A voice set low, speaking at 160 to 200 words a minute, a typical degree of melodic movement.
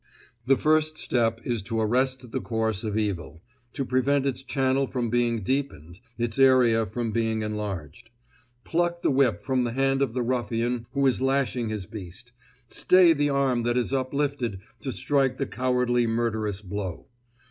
Yes: low, 120 Hz; average, 165 wpm; average, 3.4 semitones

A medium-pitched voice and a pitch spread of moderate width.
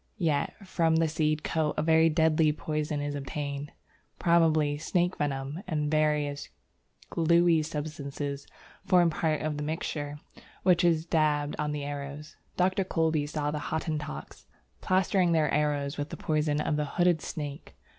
No: medium, 155 Hz; narrow, 1.8 semitones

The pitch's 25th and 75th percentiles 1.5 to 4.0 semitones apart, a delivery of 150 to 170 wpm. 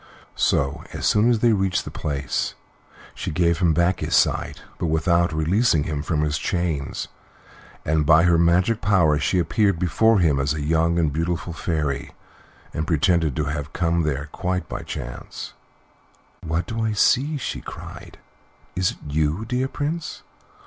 Yes: average, 3.4 semitones; average, 165 wpm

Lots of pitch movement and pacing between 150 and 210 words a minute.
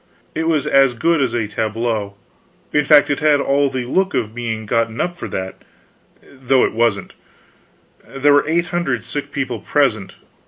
No: average, 4.4 semitones; average, 170 wpm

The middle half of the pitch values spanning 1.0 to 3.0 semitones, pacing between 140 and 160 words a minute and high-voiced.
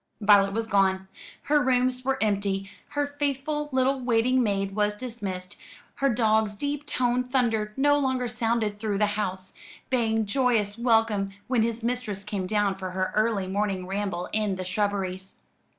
No: average, 4.1 semitones; average, 155 wpm; high, 215 Hz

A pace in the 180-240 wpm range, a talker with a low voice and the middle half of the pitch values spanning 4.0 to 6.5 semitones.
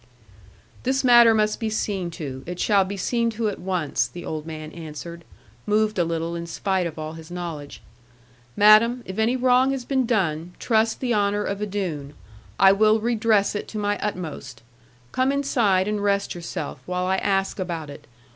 No: average, 185 wpm; high, 195 Hz; average, 4.5 semitones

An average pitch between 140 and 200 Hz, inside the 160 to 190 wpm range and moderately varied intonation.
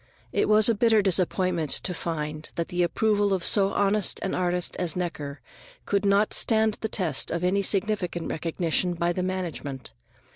Yes: medium, 185 Hz; average, 170 wpm; average, 3.2 semitones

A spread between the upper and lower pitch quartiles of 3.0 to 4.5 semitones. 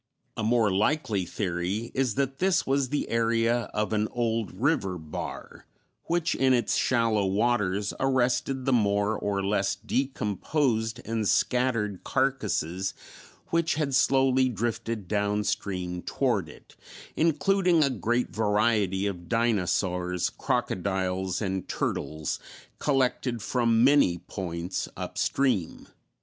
No: average, 4.9 semitones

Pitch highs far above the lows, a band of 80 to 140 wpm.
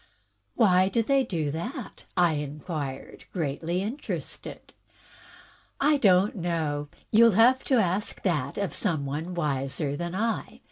Yes: wide, 6.4 semitones; slow, 135 wpm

